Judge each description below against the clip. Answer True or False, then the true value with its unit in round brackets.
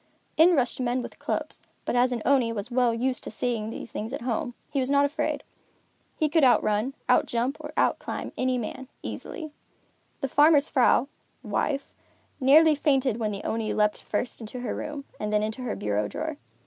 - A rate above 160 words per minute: True (180 wpm)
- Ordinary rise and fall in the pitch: True (3.5 semitones)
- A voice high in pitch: True (250 Hz)